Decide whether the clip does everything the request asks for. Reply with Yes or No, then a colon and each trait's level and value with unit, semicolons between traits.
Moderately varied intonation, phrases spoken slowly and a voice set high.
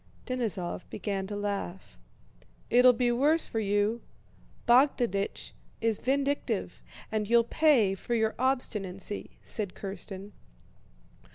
Yes: average, 3.8 semitones; slow, 105 wpm; high, 220 Hz